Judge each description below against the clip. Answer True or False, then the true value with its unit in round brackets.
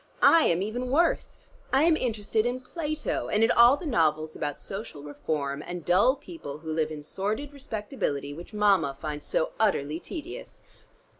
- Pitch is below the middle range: False (205 Hz)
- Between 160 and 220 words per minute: True (165 wpm)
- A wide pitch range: True (8.8 semitones)